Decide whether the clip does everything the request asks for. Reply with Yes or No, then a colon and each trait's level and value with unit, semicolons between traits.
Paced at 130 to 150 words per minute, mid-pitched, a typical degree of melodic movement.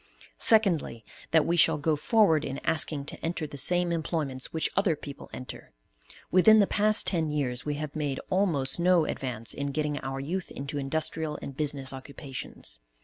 No: average, 170 wpm; medium, 150 Hz; average, 3.7 semitones